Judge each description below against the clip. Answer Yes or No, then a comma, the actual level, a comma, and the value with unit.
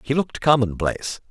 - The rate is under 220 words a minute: Yes, average, 140 wpm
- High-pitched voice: No, low, 125 Hz